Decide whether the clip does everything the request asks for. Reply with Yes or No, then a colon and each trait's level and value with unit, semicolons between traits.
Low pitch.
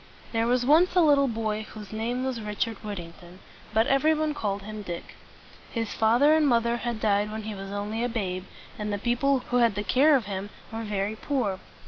No: high, 225 Hz